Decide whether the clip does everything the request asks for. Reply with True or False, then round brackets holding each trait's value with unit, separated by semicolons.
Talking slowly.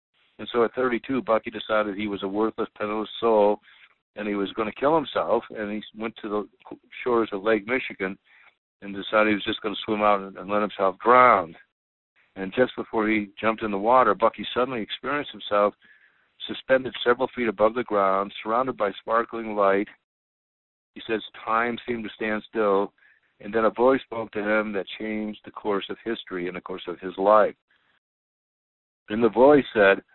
False (185 wpm)